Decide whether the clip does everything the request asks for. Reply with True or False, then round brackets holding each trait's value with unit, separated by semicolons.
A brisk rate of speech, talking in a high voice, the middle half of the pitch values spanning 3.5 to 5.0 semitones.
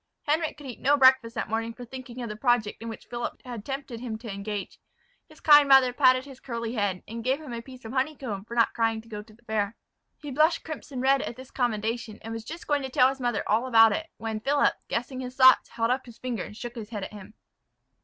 False (250 wpm; 240 Hz; 2.9 semitones)